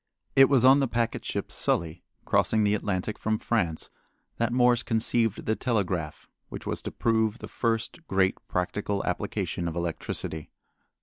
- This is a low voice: Yes, low, 110 Hz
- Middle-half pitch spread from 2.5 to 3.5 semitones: No, average, 4.3 semitones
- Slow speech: No, average, 150 wpm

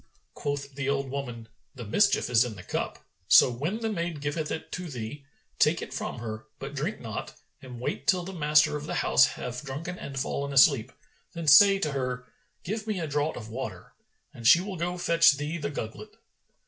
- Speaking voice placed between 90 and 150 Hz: Yes, medium, 140 Hz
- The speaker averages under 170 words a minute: No, fast, 205 wpm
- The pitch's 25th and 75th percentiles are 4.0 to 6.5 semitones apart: Yes, average, 5.0 semitones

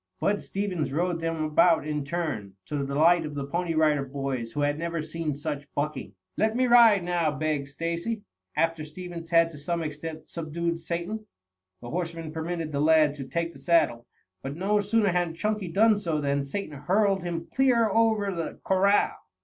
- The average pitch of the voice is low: No, medium, 165 Hz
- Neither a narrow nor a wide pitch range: Yes, average, 3.4 semitones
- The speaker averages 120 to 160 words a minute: No, average, 185 wpm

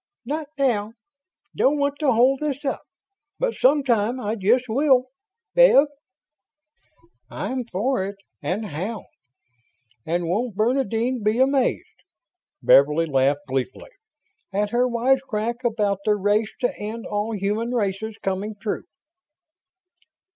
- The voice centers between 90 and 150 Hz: No, high, 225 Hz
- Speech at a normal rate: No, slow, 120 wpm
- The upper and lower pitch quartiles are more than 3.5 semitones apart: Yes, average, 4.1 semitones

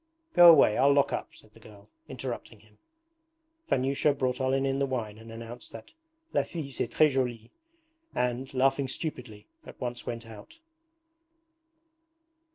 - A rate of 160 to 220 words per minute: No, average, 145 wpm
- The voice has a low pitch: Yes, low, 125 Hz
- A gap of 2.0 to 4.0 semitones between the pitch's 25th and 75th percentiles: Yes, average, 3.1 semitones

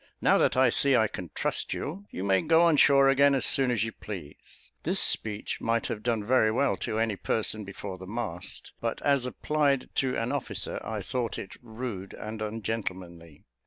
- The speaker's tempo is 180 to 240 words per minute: Yes, average, 195 wpm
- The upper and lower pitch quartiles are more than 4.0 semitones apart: Yes, average, 4.4 semitones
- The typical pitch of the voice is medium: No, low, 115 Hz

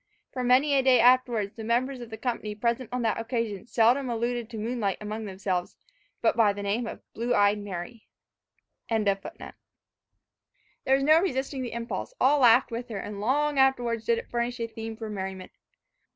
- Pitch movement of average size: Yes, average, 3.0 semitones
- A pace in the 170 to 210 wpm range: Yes, average, 180 wpm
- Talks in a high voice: Yes, high, 235 Hz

